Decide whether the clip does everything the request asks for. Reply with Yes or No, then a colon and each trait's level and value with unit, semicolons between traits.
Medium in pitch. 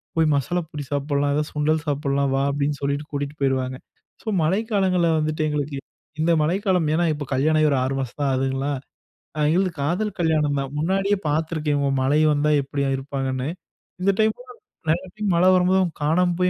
Yes: medium, 150 Hz